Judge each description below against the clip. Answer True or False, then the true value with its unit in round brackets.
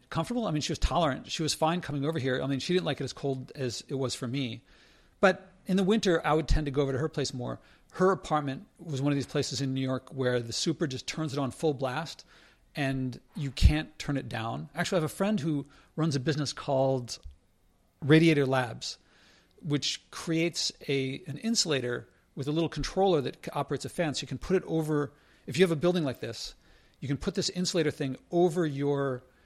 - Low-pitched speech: False (145 Hz)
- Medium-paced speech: False (225 wpm)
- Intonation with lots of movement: False (3.8 semitones)